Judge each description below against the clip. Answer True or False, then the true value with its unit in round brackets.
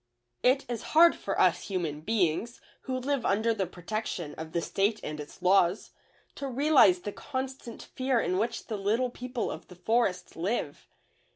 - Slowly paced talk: False (170 wpm)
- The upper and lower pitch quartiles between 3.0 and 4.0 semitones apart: False (5.6 semitones)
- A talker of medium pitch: False (220 Hz)